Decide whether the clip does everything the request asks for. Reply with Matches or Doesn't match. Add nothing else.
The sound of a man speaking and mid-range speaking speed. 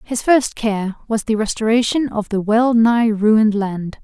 Doesn't match